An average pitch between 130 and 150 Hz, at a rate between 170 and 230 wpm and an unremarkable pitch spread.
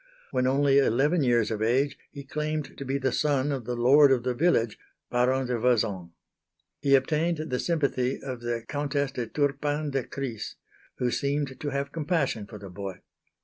Yes: low, 135 Hz; average, 180 wpm; average, 3.0 semitones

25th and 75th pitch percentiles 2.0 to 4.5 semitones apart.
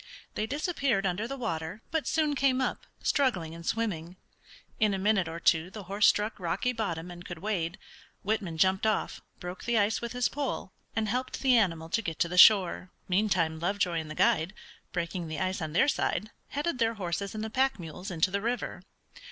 No: average, 4.9 semitones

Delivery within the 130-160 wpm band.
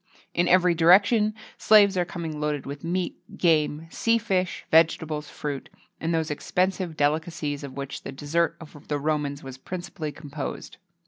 Yes: average, 150 wpm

